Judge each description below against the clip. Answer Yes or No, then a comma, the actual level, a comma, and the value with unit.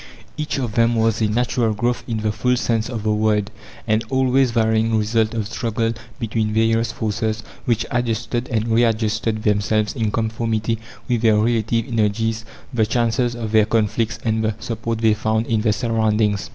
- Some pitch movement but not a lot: No, narrow, 1.3 semitones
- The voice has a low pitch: Yes, low, 110 Hz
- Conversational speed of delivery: Yes, average, 175 wpm